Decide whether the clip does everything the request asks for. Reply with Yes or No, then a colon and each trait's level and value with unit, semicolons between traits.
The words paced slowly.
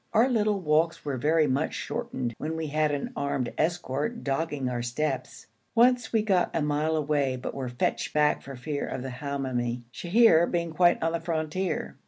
No: average, 185 wpm